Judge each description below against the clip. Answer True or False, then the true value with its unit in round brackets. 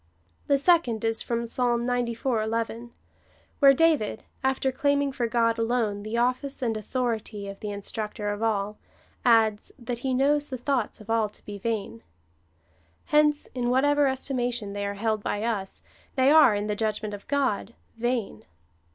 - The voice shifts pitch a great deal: False (3.6 semitones)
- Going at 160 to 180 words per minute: True (165 wpm)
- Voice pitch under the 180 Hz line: False (235 Hz)